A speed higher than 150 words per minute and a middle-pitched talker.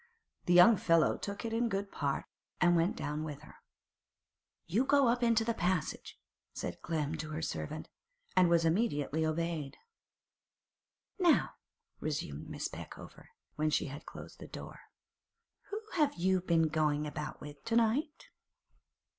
No: average, 145 wpm; medium, 170 Hz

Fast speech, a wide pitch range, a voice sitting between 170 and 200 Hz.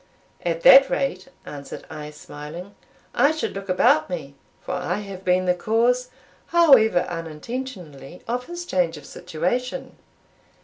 No: slow, 135 wpm; wide, 7.3 semitones; medium, 185 Hz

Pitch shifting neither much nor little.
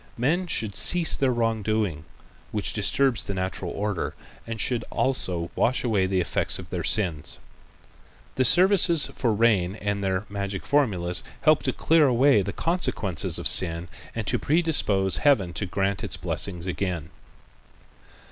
No: wide, 5.8 semitones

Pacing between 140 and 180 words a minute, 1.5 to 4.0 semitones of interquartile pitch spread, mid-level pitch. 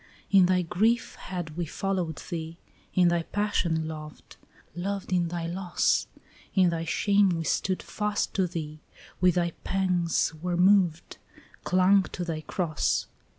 Yes: average, 145 wpm; narrow, 2.4 semitones; medium, 175 Hz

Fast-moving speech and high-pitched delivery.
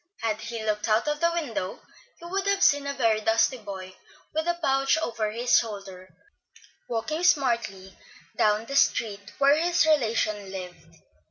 No: average, 160 wpm; high, 230 Hz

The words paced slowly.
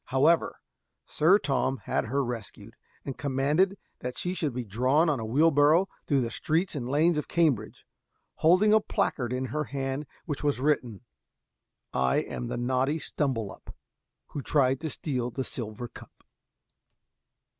No: average, 155 wpm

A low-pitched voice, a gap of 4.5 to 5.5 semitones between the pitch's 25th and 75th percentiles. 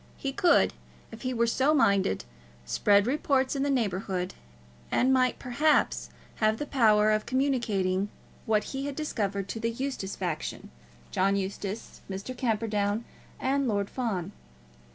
No: high, 225 Hz; average, 4.8 semitones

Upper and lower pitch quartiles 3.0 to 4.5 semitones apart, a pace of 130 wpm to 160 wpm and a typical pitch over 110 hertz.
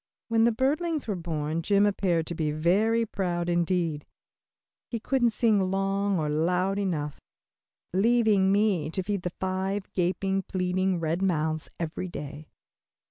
Yes: average, 3.4 semitones; average, 140 wpm; medium, 185 Hz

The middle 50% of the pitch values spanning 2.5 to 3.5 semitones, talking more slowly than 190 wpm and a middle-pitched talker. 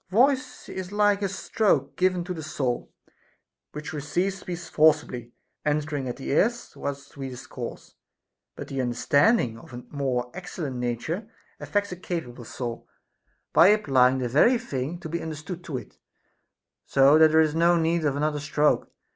No: average, 5.2 semitones; average, 160 wpm; medium, 155 Hz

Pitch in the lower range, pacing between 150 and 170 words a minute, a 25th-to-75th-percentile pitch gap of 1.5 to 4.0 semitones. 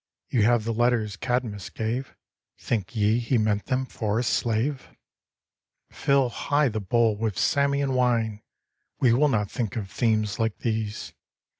Yes: low, 115 Hz; average, 155 wpm; average, 2.7 semitones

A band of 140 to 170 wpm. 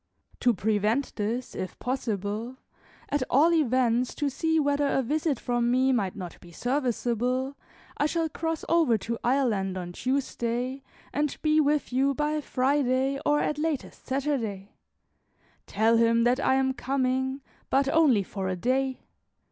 Yes: average, 150 wpm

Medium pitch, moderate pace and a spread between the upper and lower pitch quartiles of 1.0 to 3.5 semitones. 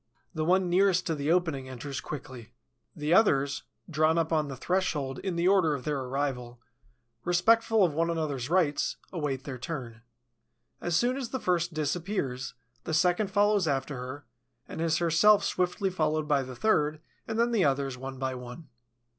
No: medium, 155 Hz; average, 170 wpm; average, 5.0 semitones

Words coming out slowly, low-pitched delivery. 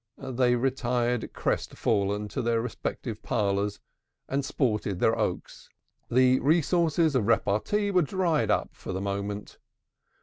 Yes: slow, 125 wpm; low, 120 Hz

